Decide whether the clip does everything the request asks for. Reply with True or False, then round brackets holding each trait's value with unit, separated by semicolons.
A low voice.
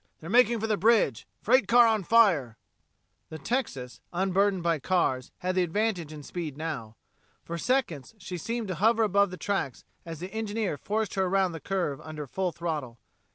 False (185 Hz)